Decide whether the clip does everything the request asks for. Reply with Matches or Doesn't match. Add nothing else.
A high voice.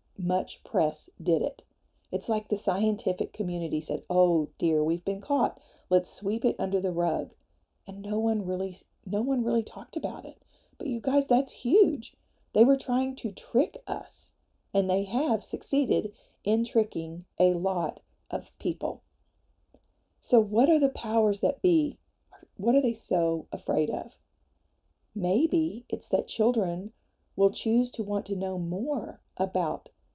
Matches